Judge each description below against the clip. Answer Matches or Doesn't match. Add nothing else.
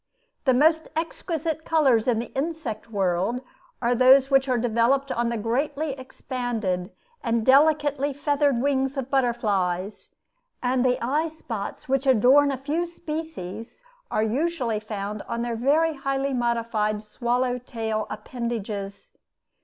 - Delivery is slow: Matches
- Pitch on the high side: Matches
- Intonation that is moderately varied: Matches